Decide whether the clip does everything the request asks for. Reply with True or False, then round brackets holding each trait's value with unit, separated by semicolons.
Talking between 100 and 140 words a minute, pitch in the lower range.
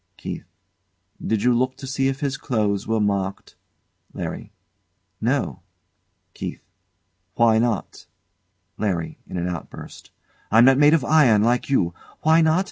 True (135 wpm; 120 Hz)